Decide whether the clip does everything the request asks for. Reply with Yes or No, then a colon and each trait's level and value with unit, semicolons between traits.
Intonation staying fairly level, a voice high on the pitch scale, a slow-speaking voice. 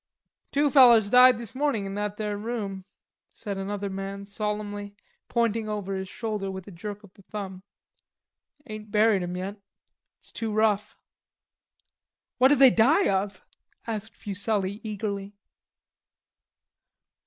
Yes: narrow, 2.1 semitones; high, 210 Hz; slow, 130 wpm